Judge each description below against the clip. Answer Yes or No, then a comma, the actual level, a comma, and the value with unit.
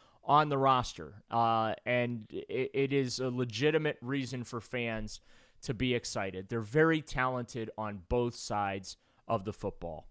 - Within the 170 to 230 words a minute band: No, average, 150 wpm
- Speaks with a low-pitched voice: Yes, low, 120 Hz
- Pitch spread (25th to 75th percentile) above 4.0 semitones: No, average, 3.2 semitones